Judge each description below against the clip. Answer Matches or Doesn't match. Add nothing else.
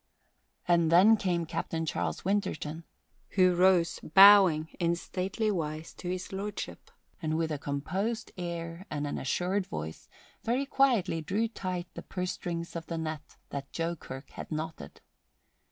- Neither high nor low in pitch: Matches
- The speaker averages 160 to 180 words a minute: Doesn't match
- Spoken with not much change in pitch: Doesn't match